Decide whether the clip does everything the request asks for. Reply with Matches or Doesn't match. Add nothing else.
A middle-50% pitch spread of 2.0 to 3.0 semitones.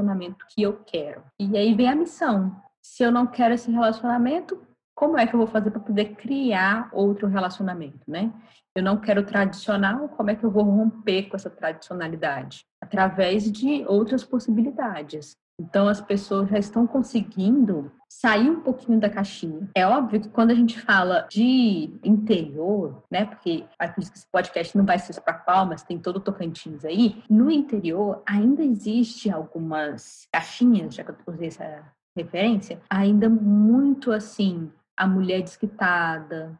Doesn't match